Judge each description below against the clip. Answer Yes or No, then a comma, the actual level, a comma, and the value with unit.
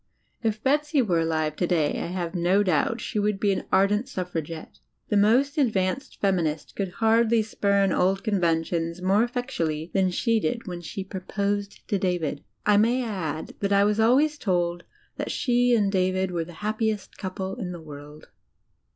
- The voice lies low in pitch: No, high, 195 Hz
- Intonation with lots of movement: No, average, 4.0 semitones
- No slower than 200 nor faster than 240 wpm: No, average, 170 wpm